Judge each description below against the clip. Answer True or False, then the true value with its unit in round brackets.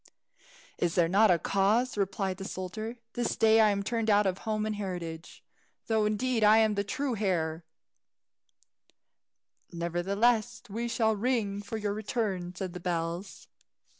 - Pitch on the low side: False (205 Hz)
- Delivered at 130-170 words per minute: True (150 wpm)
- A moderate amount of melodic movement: True (3.2 semitones)